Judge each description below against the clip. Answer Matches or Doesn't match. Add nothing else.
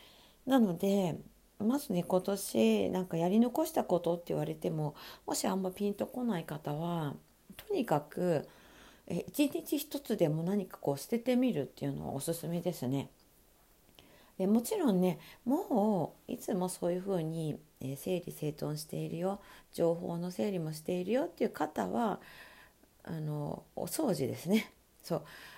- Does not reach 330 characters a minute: Matches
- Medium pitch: Matches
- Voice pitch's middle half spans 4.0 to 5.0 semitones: Doesn't match